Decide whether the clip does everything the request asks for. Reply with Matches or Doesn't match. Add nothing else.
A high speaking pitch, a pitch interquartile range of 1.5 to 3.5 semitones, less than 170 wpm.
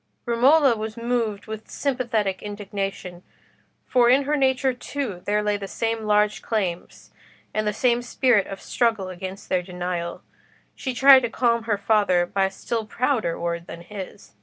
Doesn't match